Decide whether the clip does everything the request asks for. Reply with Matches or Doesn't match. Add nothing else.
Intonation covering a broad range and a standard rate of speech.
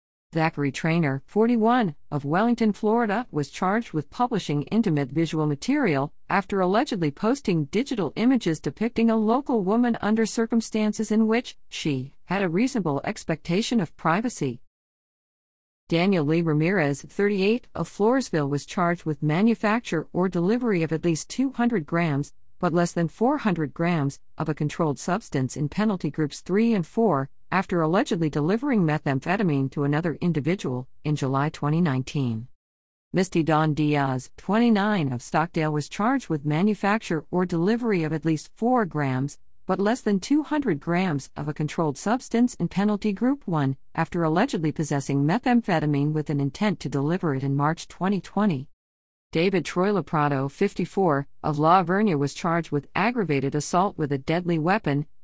Matches